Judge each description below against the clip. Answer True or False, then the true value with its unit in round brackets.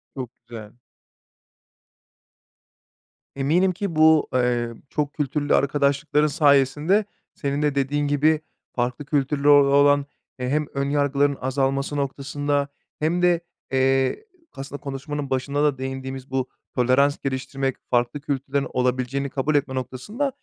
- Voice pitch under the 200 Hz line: True (140 Hz)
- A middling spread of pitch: False (1.8 semitones)